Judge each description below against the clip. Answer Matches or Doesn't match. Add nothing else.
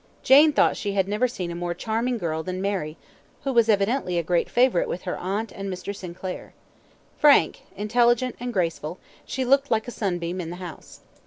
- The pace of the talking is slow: Doesn't match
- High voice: Matches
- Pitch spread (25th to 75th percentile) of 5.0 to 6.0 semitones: Matches